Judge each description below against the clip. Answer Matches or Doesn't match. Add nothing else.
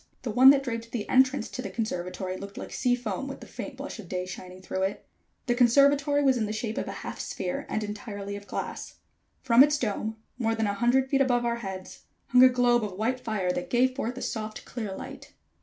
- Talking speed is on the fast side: Matches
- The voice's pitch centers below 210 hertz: Doesn't match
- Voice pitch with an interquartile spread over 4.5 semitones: Doesn't match